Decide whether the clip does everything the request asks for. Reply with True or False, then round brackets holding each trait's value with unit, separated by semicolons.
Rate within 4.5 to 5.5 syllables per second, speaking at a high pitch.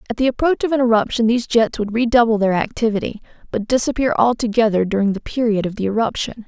False (6.5 syllables/s; 225 Hz)